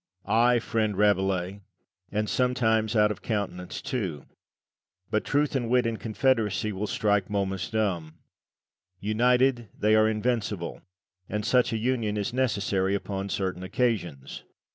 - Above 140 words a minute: No, slow, 135 wpm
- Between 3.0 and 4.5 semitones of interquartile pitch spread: Yes, average, 3.3 semitones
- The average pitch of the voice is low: Yes, low, 105 Hz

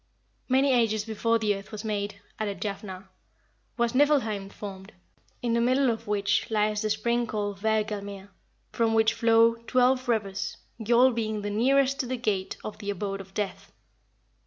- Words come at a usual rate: Yes, average, 165 wpm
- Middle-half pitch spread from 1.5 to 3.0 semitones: Yes, narrow, 2.6 semitones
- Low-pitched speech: No, high, 215 Hz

